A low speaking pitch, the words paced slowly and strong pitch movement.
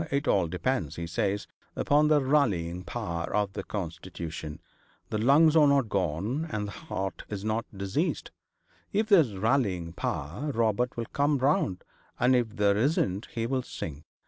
No: low, 110 Hz; average, 155 wpm; wide, 6.9 semitones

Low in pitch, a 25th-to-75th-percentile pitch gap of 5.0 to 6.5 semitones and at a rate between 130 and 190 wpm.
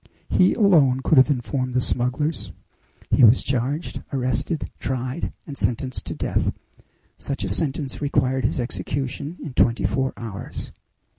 No: low, 130 Hz; narrow, 2.4 semitones; average, 140 wpm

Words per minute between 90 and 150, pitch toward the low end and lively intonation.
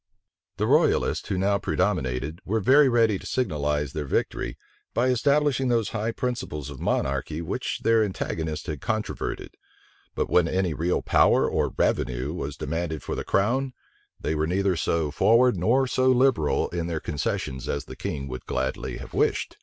No: average, 165 wpm; very low, 90 Hz; wide, 7.8 semitones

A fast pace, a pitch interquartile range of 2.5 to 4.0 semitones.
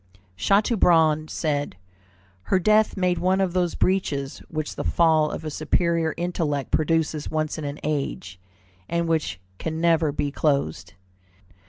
No: average, 140 wpm; average, 2.8 semitones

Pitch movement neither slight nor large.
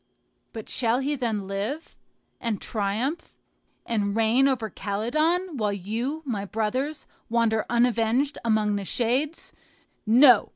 Yes: average, 4.1 semitones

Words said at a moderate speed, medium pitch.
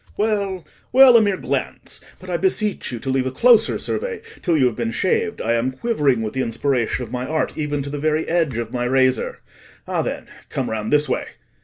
No: fast, 215 wpm; medium, 145 Hz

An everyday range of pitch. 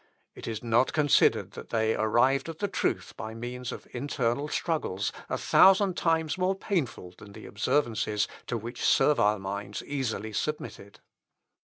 No: wide, 5.7 semitones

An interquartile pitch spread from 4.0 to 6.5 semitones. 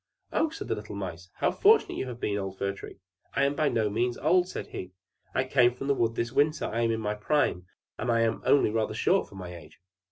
Yes: average, 5.3 semitones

